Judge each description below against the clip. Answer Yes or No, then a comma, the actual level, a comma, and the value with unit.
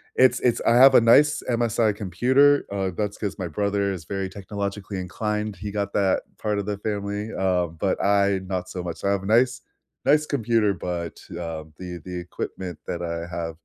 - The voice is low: Yes, low, 100 Hz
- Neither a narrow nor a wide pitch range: Yes, average, 3.0 semitones